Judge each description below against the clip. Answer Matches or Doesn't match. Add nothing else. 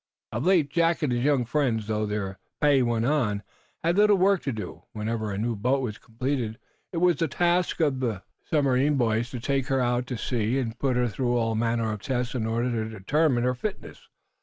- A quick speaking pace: Matches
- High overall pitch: Doesn't match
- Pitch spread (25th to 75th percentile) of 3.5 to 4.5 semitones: Matches